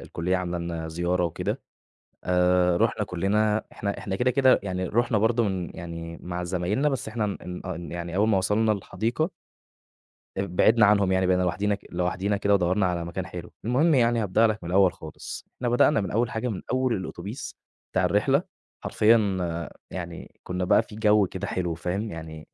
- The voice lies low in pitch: Yes, very low, 95 Hz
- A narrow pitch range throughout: No, average, 3.7 semitones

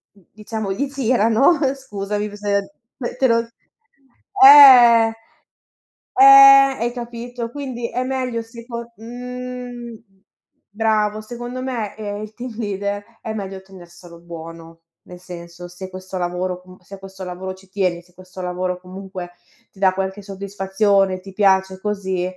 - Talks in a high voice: Yes, high, 205 Hz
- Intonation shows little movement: No, average, 4.0 semitones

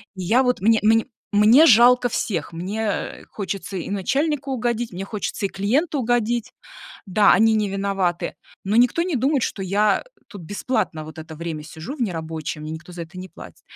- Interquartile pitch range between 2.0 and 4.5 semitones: No, average, 5.3 semitones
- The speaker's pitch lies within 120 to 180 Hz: No, high, 205 Hz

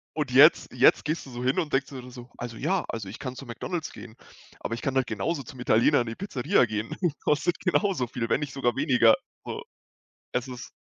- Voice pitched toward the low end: Yes, low, 130 Hz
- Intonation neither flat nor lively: Yes, average, 3.4 semitones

